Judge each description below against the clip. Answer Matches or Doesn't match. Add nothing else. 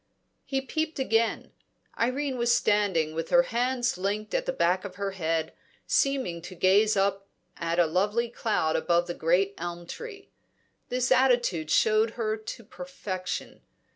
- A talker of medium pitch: Doesn't match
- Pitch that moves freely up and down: Matches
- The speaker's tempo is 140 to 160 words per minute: Matches